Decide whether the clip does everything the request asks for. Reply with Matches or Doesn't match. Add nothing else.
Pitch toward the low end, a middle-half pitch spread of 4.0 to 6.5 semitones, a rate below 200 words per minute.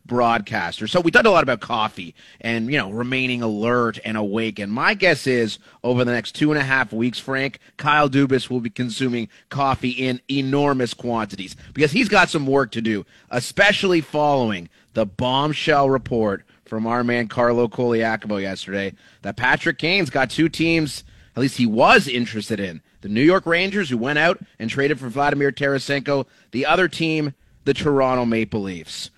Matches